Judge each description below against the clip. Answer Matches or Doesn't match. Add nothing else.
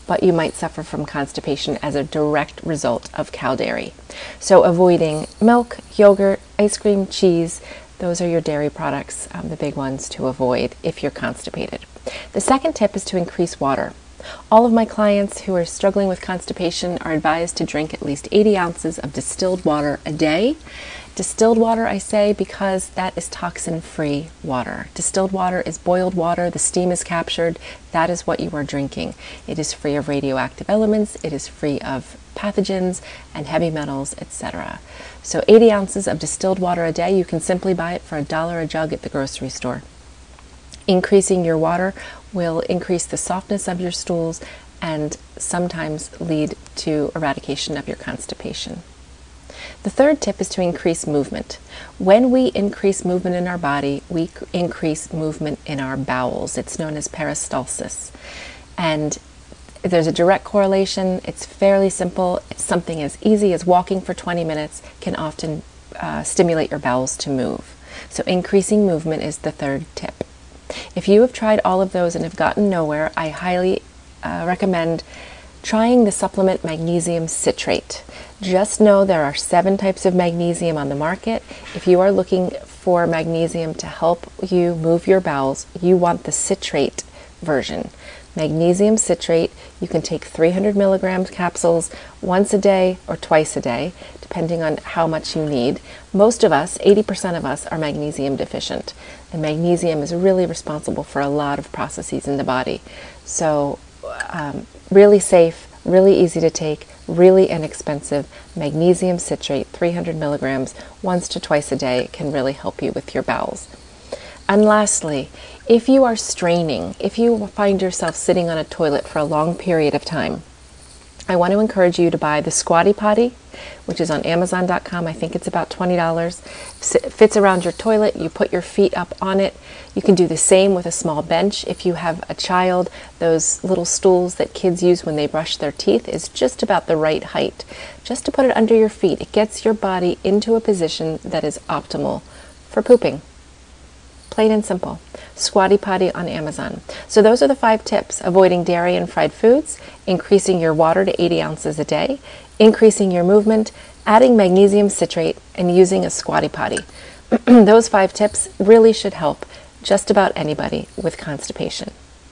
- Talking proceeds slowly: Doesn't match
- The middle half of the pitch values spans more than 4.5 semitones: Doesn't match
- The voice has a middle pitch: Matches